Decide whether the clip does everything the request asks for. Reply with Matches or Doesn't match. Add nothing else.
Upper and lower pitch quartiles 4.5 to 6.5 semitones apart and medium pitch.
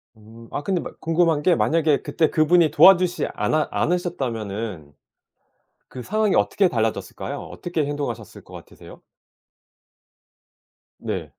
Doesn't match